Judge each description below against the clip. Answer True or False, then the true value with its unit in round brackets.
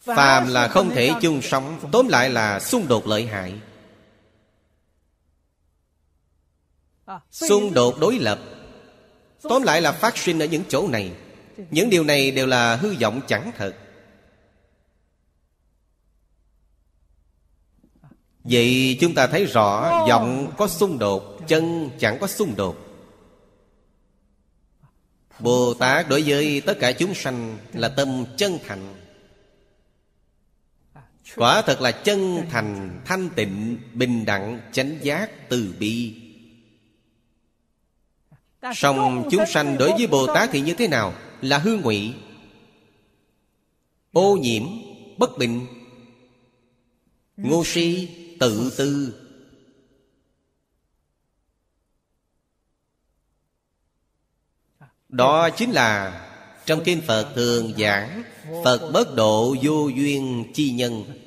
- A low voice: True (120 Hz)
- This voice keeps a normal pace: False (110 wpm)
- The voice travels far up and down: True (6.7 semitones)